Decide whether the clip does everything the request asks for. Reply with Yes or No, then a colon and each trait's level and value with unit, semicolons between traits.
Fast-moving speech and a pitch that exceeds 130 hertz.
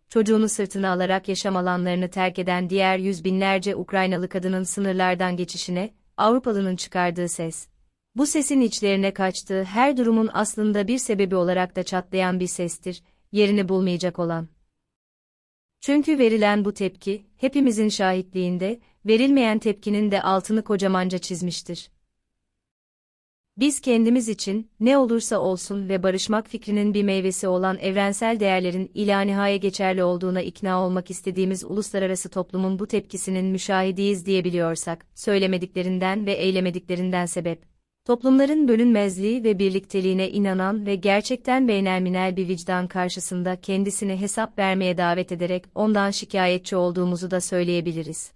No: average, 120 wpm; high, 190 Hz